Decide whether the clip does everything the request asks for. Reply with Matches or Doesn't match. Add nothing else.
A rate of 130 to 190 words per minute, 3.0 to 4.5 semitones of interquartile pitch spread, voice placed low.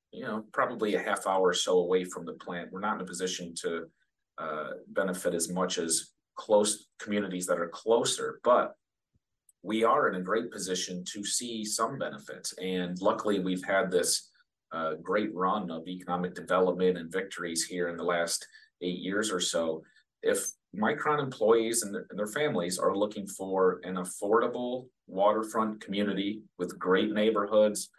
Matches